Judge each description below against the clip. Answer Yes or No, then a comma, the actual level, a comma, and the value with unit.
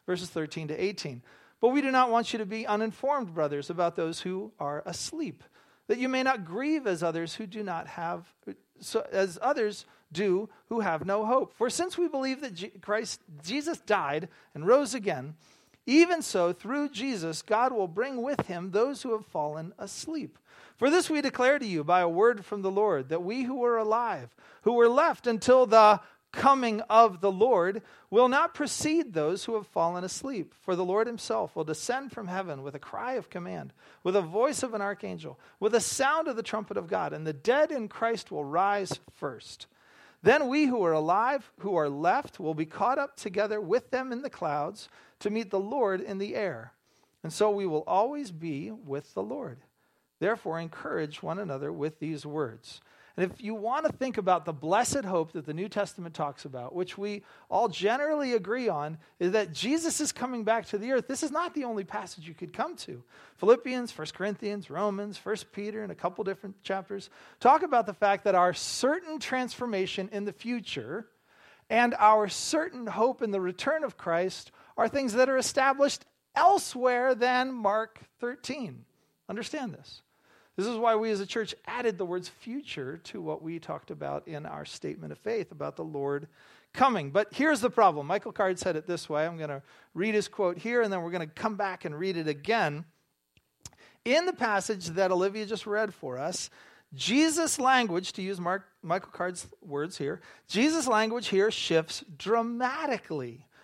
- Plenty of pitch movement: Yes, wide, 5.8 semitones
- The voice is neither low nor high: No, high, 210 Hz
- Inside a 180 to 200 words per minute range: Yes, average, 195 wpm